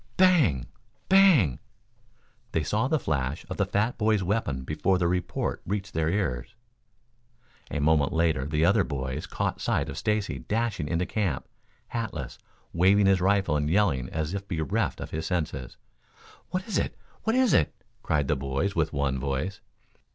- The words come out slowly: No, average, 160 wpm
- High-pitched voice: No, very low, 85 Hz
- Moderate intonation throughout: No, wide, 5.9 semitones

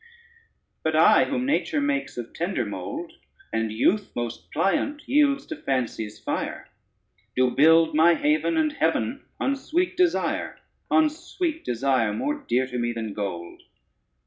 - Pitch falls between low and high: Yes, medium, 170 Hz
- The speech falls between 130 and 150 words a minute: Yes, average, 145 wpm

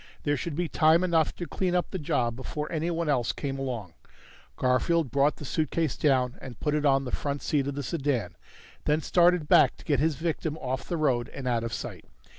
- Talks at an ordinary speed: No, fast, 215 wpm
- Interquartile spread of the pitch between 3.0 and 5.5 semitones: Yes, average, 3.7 semitones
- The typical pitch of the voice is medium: Yes, medium, 145 Hz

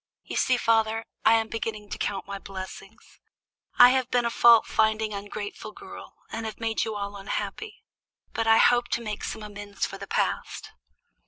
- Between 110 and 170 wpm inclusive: No, average, 180 wpm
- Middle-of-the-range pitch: No, high, 220 Hz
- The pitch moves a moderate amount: No, narrow, 1.8 semitones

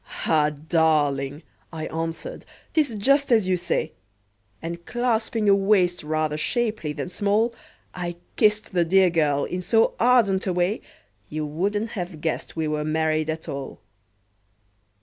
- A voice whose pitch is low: No, medium, 175 Hz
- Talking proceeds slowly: No, average, 145 wpm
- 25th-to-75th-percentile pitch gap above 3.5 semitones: Yes, average, 5.1 semitones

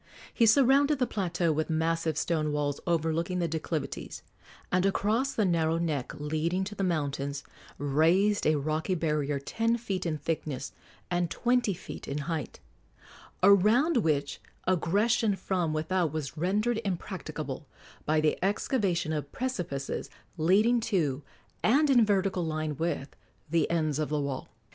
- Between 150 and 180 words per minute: No, average, 140 wpm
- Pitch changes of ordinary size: Yes, average, 4.7 semitones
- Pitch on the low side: No, medium, 170 Hz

